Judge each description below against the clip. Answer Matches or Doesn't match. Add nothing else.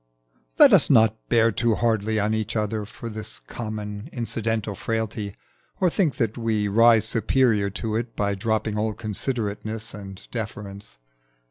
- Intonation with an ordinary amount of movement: Doesn't match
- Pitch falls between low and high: Doesn't match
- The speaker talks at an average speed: Matches